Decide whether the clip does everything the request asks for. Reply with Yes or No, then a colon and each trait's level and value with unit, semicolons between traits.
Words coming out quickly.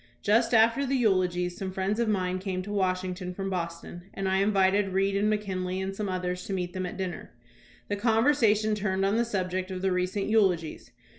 Yes: fast, 210 wpm